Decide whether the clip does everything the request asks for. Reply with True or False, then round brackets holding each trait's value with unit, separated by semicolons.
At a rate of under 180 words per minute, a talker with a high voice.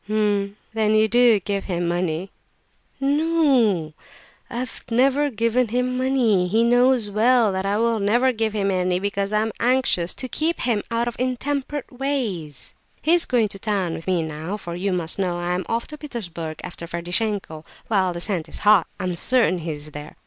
False (195 wpm; 210 Hz)